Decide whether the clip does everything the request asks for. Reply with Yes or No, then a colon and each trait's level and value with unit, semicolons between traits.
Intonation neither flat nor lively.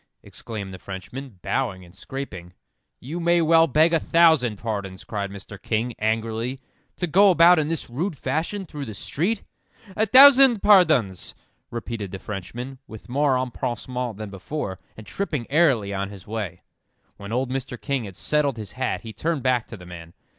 No: wide, 7.3 semitones